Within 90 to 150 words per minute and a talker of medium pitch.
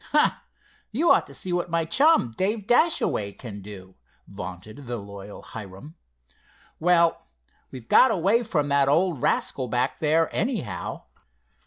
Yes: average, 140 wpm; medium, 145 Hz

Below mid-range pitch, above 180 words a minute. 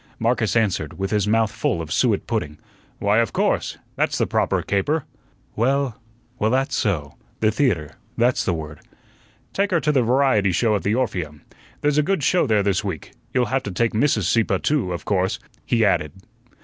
Yes: low, 110 Hz; average, 190 wpm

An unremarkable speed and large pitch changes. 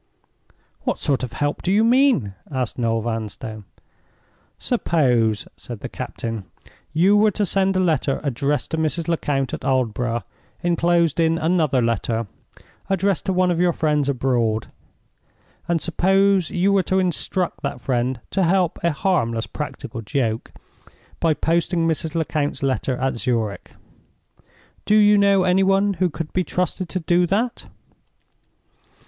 Yes: average, 145 wpm; wide, 6.5 semitones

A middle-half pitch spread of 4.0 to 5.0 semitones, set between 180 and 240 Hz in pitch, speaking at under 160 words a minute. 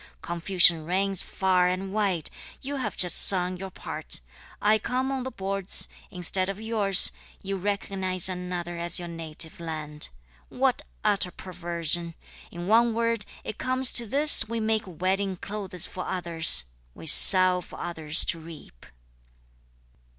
No: average, 3.0 semitones; medium, 185 Hz; average, 145 wpm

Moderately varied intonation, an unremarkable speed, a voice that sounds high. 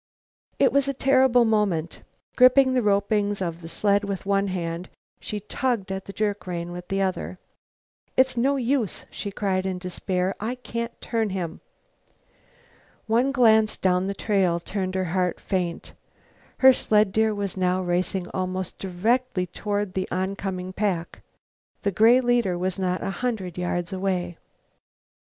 Yes: average, 3.4 semitones; average, 150 wpm; high, 195 Hz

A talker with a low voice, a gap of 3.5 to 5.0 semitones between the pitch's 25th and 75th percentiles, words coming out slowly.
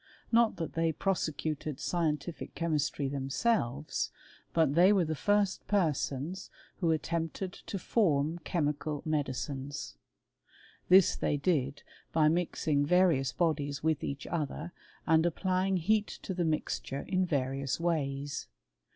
No: medium, 160 Hz; average, 3.8 semitones; slow, 125 wpm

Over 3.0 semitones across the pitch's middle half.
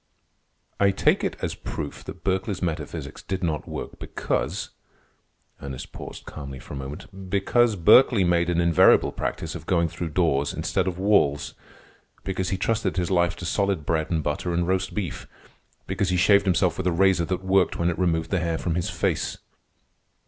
No: narrow, 2.6 semitones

